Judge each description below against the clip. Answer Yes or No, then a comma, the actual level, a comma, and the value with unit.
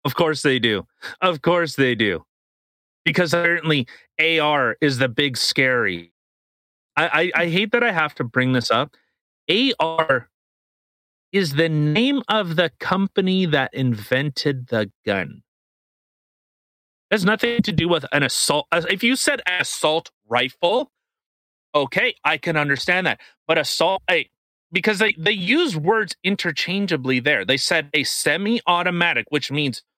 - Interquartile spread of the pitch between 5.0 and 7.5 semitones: Yes, wide, 5.5 semitones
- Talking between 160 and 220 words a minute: No, average, 145 wpm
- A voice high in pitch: No, medium, 165 Hz